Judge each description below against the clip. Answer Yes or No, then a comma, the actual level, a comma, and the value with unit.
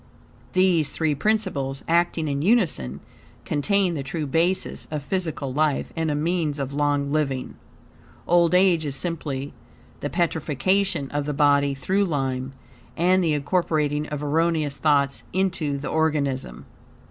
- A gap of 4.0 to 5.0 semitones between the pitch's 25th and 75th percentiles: No, average, 3.4 semitones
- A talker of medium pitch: Yes, medium, 150 Hz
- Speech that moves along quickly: No, slow, 135 wpm